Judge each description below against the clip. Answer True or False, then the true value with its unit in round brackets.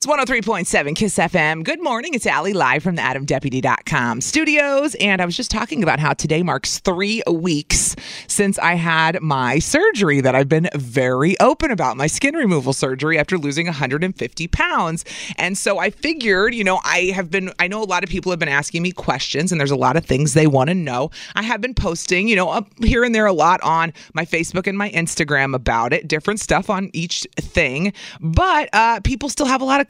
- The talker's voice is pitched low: False (175 Hz)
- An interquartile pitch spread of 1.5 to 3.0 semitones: False (5.6 semitones)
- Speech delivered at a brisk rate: True (215 wpm)